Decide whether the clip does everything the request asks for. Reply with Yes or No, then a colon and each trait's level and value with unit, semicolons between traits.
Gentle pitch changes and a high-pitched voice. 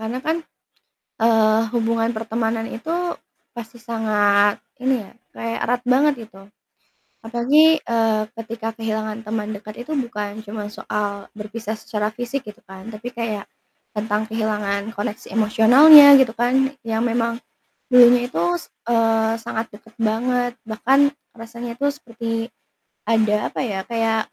Yes: narrow, 1.7 semitones; high, 225 Hz